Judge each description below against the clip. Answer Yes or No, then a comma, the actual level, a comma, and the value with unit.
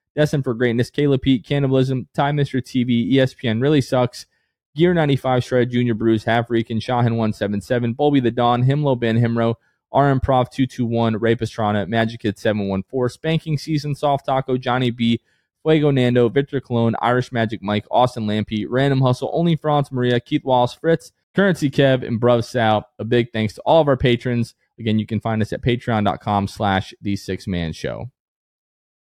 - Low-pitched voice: Yes, low, 120 Hz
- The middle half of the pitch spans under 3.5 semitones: Yes, average, 3.1 semitones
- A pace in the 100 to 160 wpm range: No, average, 170 wpm